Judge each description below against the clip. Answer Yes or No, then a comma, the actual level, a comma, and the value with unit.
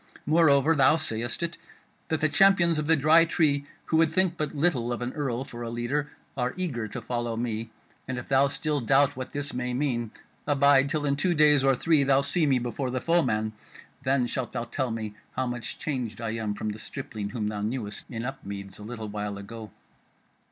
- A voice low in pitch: Yes, low, 130 Hz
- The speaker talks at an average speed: No, fast, 210 wpm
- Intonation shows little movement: No, average, 4.2 semitones